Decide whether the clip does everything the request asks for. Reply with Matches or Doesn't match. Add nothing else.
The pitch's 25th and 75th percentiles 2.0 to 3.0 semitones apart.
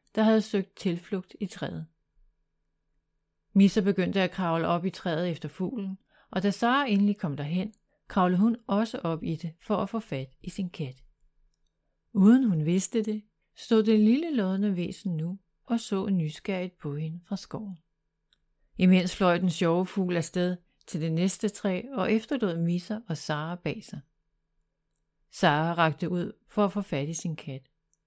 Doesn't match